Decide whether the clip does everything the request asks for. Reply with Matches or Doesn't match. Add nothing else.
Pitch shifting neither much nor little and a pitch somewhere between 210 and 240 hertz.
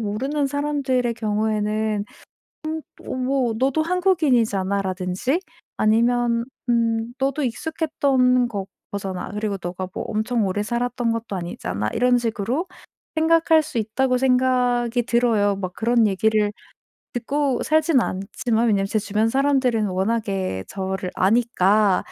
Matches